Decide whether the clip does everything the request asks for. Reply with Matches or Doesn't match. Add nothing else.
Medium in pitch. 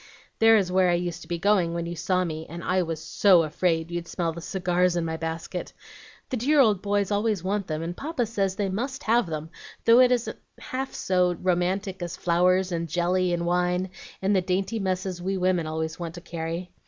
Matches